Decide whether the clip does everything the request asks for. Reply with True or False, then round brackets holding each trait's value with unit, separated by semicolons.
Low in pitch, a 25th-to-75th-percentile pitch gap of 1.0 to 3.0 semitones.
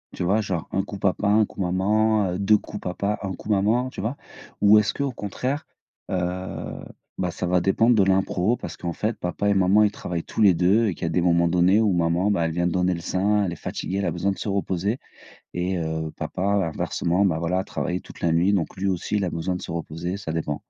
True (95 Hz; 2.7 semitones)